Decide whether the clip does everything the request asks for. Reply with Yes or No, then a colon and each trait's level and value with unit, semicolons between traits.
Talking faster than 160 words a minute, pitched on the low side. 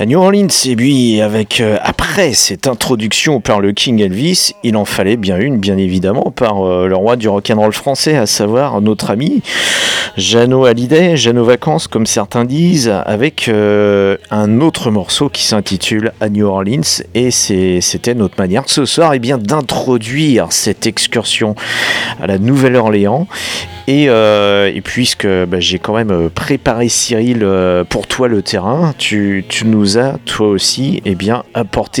Yes: average, 170 wpm; low, 110 Hz